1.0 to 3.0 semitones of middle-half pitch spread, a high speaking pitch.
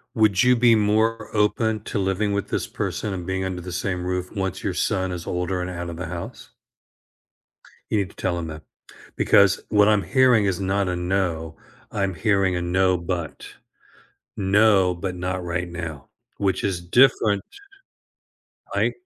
No: narrow, 2.5 semitones; very low, 95 Hz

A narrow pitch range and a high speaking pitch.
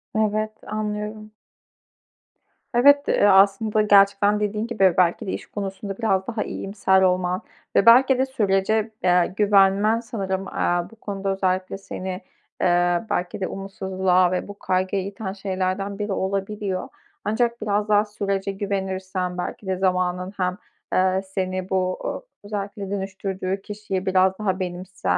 Yes: narrow, 1.9 semitones; high, 195 Hz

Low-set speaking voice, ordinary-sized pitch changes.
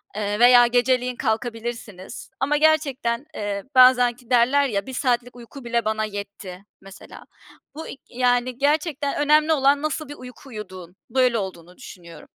No: high, 245 Hz; average, 4.1 semitones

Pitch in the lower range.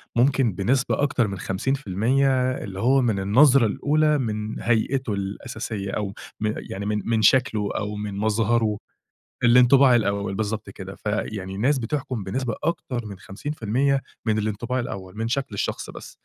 Yes: low, 110 Hz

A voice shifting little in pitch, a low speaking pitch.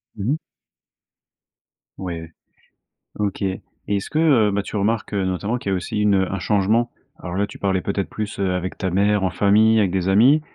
Yes: narrow, 2.1 semitones; low, 100 Hz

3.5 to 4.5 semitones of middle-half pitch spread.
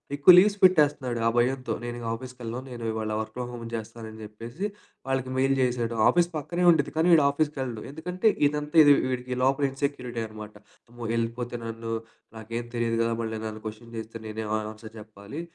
Yes: average, 3.8 semitones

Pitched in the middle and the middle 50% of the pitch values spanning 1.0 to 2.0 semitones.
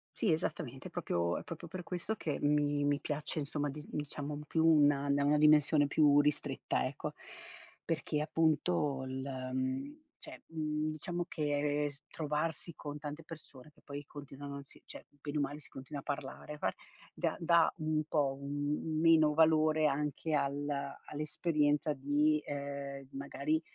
Yes: medium, 150 Hz; narrow, 1.5 semitones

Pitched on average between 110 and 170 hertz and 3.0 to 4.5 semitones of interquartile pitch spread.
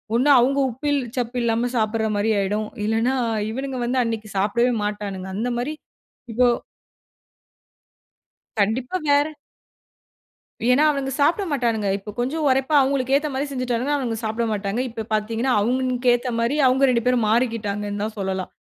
No: high, 240 Hz; average, 3.4 semitones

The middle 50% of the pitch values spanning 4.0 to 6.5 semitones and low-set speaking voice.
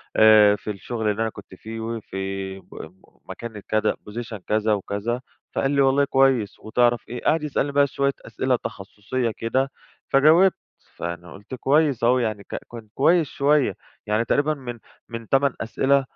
Yes: average, 4.4 semitones; low, 120 Hz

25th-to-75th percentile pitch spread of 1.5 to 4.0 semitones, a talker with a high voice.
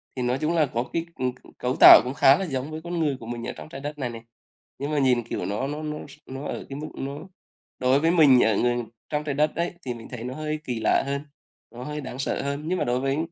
No: average, 3.3 semitones; low, 135 Hz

